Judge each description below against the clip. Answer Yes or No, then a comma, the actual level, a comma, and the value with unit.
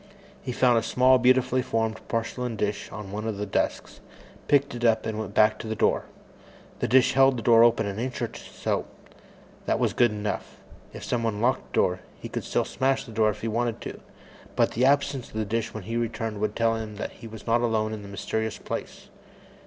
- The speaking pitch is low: Yes, low, 115 Hz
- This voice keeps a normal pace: No, fast, 225 wpm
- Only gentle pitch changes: Yes, narrow, 2.1 semitones